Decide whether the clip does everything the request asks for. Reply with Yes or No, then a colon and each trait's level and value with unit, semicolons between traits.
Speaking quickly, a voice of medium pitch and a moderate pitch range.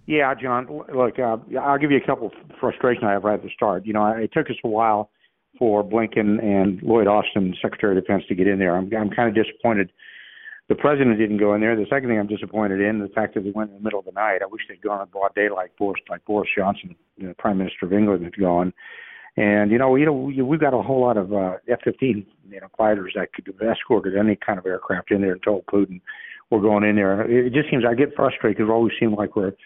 No: fast, 275 wpm; low, 105 Hz; average, 3.6 semitones